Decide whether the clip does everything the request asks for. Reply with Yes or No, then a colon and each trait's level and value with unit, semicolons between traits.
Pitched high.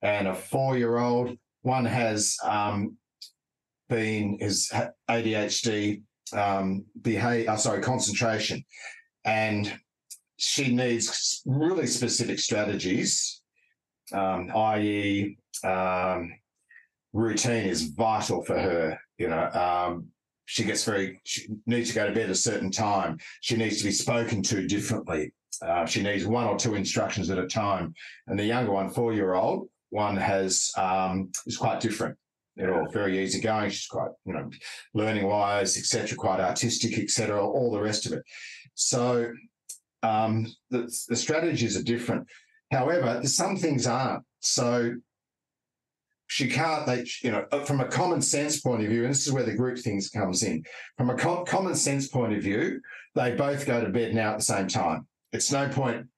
No: low, 115 Hz